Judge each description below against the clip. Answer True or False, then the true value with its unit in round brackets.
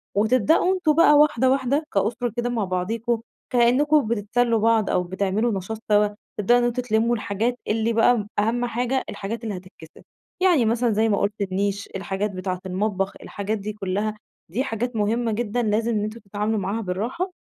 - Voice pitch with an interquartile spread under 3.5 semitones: True (3.0 semitones)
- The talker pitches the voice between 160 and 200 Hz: False (220 Hz)